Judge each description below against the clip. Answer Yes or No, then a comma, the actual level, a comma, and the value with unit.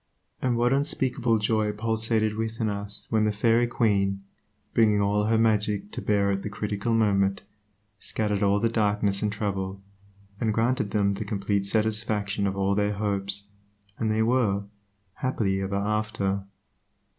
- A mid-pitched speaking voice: No, low, 105 Hz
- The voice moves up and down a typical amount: No, narrow, 1.9 semitones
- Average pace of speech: Yes, average, 150 wpm